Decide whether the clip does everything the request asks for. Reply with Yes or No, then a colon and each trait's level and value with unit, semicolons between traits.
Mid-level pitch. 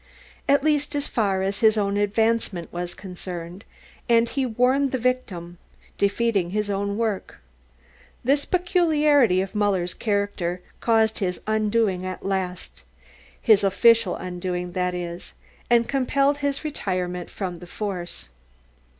No: high, 205 Hz